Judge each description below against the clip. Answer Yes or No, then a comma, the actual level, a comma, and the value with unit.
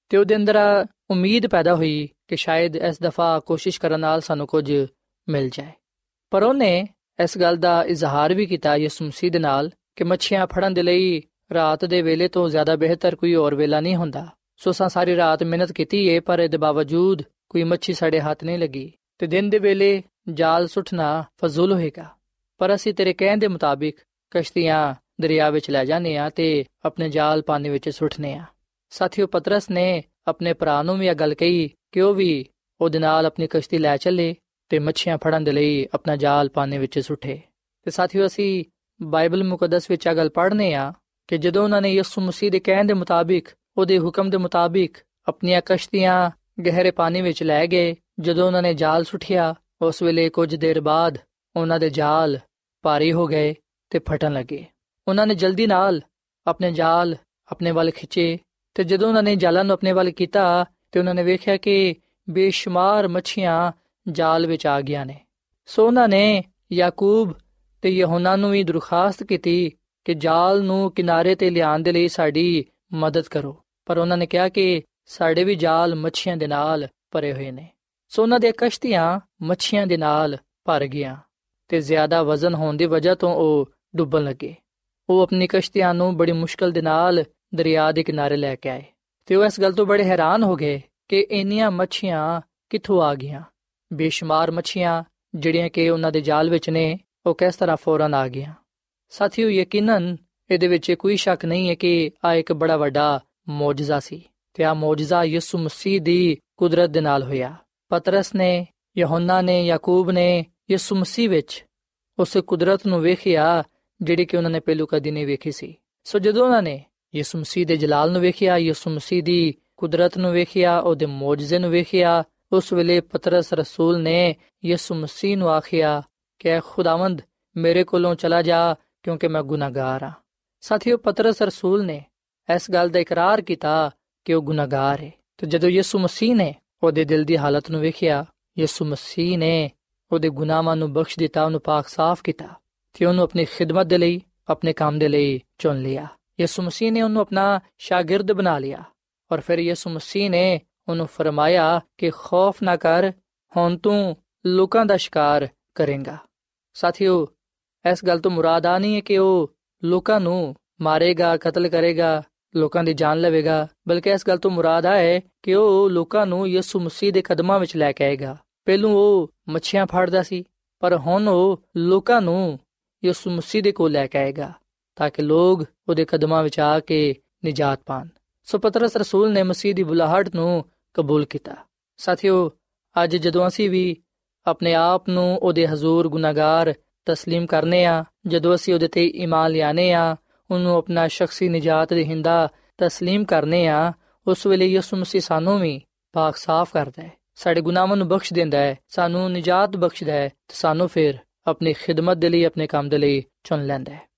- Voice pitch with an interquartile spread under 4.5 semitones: Yes, average, 2.7 semitones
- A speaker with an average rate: No, fast, 170 wpm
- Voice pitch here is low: No, medium, 170 Hz